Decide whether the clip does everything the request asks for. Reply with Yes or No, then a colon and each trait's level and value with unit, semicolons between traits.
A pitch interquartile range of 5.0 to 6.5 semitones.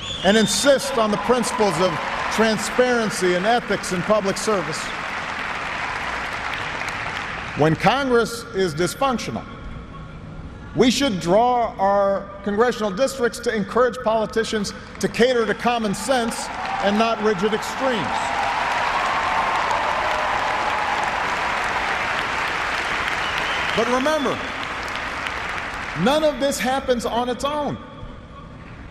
No: average, 3.8 semitones